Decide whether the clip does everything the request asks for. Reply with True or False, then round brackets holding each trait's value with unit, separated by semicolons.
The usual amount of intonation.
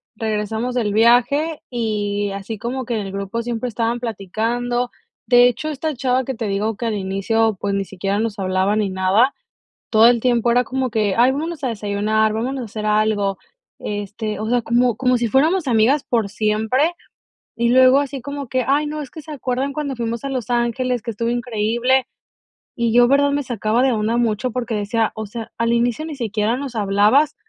True (3.1 semitones)